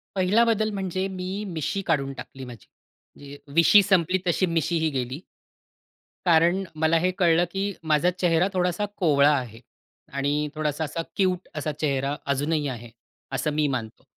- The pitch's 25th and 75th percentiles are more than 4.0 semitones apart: Yes, average, 4.5 semitones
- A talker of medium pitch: Yes, medium, 160 Hz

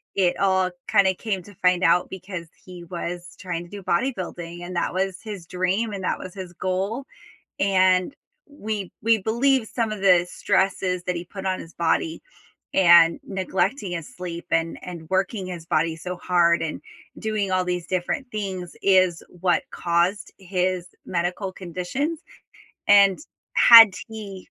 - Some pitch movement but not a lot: No, narrow, 2.2 semitones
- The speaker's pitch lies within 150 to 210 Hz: Yes, medium, 185 Hz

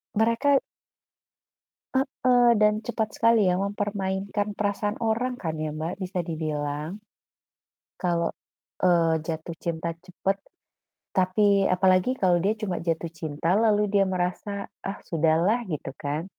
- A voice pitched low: No, high, 190 Hz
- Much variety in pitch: No, average, 3.9 semitones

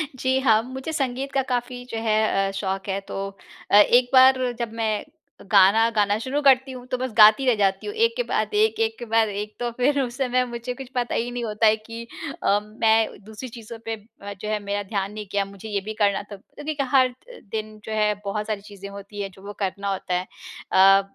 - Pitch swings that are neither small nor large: Yes, average, 3.9 semitones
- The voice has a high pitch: Yes, high, 220 Hz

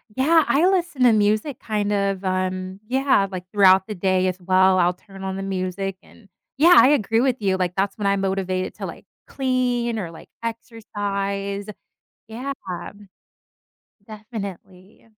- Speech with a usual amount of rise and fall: Yes, average, 3.5 semitones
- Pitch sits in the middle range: No, high, 200 Hz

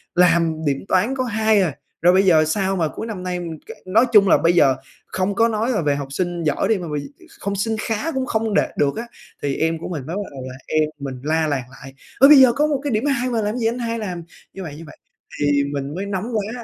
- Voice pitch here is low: No, medium, 185 Hz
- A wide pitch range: Yes, wide, 6.2 semitones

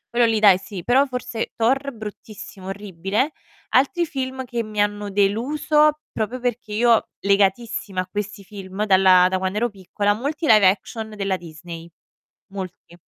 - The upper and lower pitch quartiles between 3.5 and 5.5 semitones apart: Yes, average, 4.0 semitones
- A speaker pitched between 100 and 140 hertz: No, high, 210 Hz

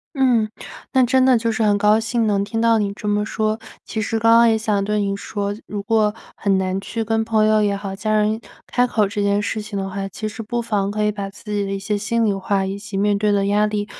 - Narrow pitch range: Yes, narrow, 1.8 semitones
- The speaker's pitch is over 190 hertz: Yes, high, 210 Hz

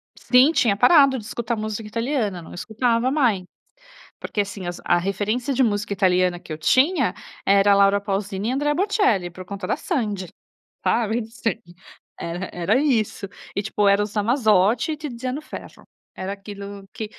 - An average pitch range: Yes, average, 4.1 semitones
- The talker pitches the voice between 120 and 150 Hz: No, high, 210 Hz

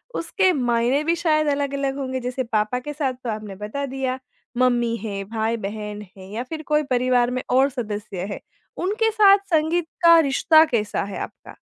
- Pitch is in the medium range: No, very high, 255 Hz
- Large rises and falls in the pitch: Yes, wide, 5.7 semitones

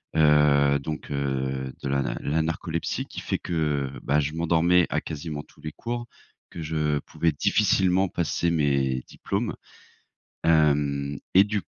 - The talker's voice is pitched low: Yes, very low, 75 Hz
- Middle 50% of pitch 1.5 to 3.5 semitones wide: Yes, average, 2.9 semitones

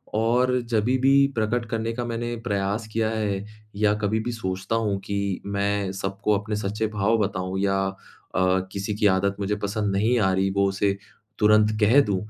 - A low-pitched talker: Yes, low, 105 Hz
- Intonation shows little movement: Yes, narrow, 2.2 semitones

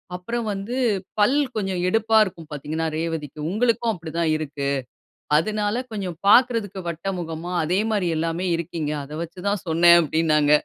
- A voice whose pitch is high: No, medium, 175 Hz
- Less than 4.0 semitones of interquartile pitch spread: No, average, 4.3 semitones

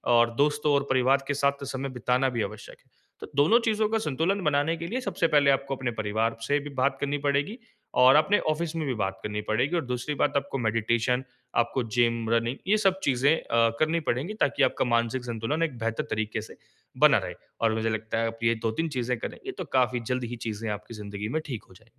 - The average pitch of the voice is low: Yes, low, 130 Hz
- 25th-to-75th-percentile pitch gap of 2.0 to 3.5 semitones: No, average, 4.3 semitones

